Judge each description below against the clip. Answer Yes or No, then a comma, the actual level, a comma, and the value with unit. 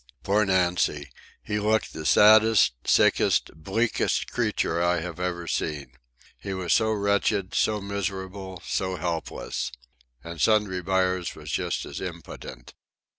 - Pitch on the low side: Yes, very low, 95 Hz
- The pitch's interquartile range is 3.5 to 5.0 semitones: No, average, 2.9 semitones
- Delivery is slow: Yes, slow, 125 wpm